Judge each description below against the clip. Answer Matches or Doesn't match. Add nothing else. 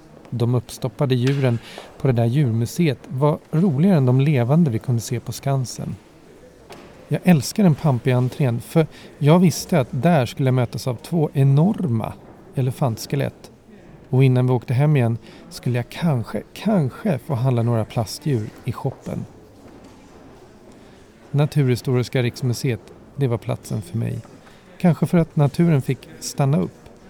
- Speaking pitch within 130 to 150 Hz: Matches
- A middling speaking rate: Matches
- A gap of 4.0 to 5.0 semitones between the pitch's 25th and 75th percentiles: Matches